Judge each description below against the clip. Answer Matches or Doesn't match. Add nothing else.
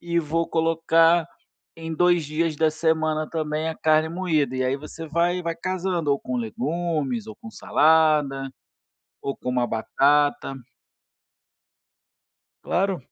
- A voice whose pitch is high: Doesn't match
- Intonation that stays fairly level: Matches